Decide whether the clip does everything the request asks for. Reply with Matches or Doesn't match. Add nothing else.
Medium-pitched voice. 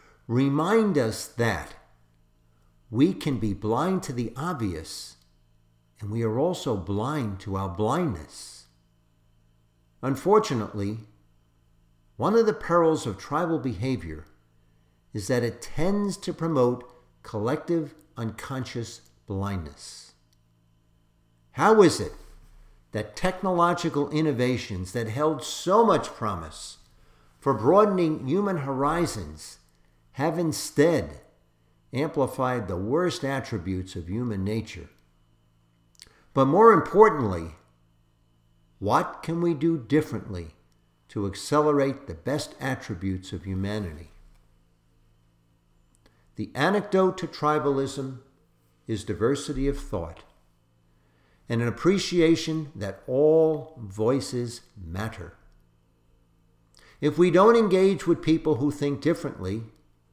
Doesn't match